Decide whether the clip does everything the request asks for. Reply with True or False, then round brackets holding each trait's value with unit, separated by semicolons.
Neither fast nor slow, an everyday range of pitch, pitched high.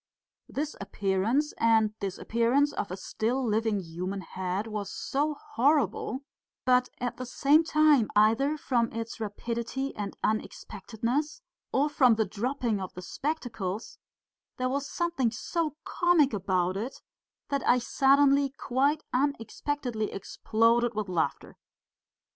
False (120 wpm; 4.8 semitones; 235 Hz)